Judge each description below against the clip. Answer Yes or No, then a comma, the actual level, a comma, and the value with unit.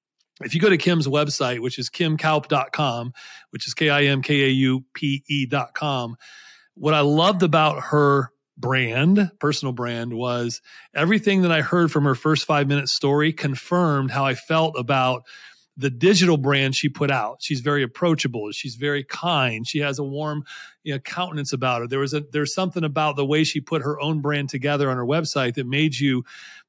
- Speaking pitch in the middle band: Yes, medium, 145 Hz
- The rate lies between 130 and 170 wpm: No, average, 190 wpm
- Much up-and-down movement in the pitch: No, narrow, 2.6 semitones